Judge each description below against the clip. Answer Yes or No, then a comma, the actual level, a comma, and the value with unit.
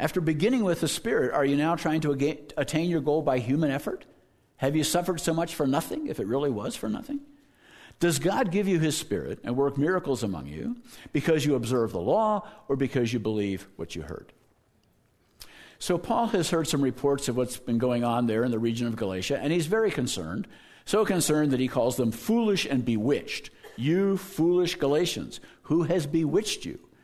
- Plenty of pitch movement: Yes, wide, 6.1 semitones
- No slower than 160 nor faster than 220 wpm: Yes, average, 200 wpm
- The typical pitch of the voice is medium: Yes, medium, 155 Hz